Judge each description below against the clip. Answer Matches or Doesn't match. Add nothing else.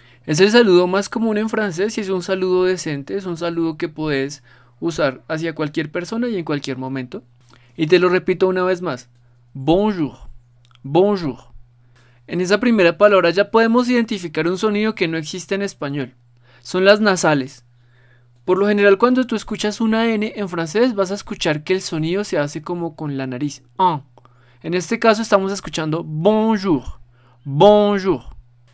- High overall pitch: Doesn't match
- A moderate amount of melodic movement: Doesn't match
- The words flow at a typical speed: Matches